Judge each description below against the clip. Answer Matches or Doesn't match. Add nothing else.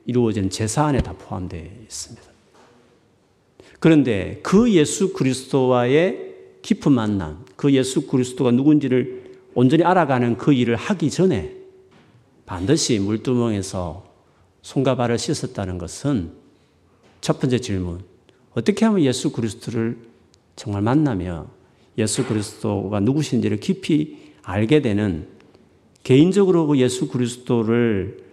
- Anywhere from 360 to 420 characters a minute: Doesn't match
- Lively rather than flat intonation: Matches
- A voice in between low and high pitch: Doesn't match